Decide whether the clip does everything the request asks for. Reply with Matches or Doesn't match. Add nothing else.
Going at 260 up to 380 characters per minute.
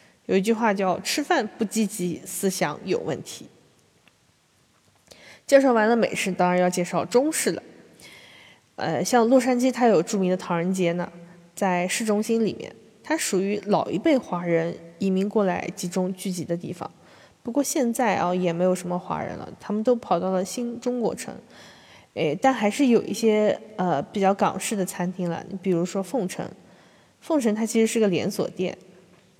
Doesn't match